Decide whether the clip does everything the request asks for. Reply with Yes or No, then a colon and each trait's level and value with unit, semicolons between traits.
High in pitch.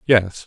No: low, 105 Hz